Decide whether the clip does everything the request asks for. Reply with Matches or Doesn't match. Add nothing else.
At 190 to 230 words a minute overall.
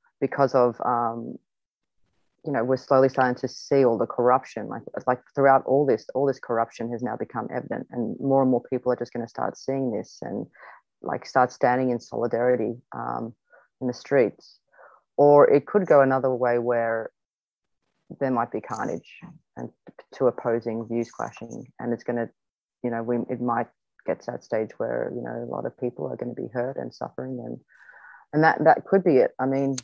Matches